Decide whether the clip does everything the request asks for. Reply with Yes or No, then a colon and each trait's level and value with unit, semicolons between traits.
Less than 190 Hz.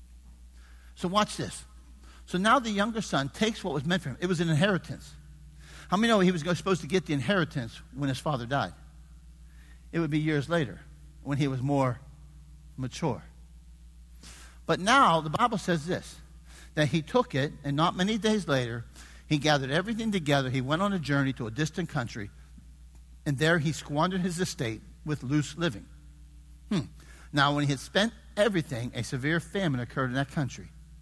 Yes: medium, 140 Hz